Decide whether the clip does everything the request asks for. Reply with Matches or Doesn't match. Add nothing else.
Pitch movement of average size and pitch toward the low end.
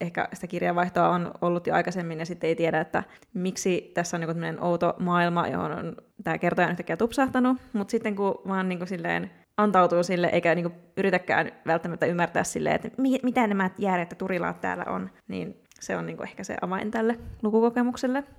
Doesn't match